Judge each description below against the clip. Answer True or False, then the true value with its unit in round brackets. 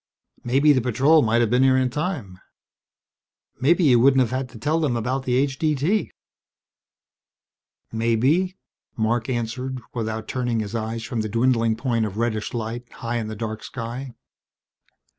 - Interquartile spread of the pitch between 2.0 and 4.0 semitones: True (2.8 semitones)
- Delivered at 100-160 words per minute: True (155 wpm)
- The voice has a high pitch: False (120 Hz)